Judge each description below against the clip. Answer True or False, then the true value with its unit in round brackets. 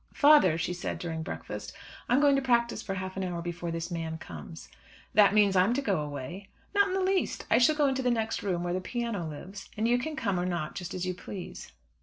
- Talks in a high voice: True (195 Hz)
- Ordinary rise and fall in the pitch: False (5.7 semitones)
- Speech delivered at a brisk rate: True (245 wpm)